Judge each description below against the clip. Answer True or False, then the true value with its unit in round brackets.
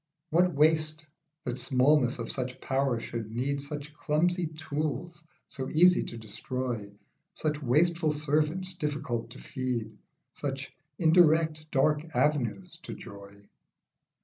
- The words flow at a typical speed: False (120 wpm)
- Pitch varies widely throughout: False (3.7 semitones)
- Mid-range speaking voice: True (150 Hz)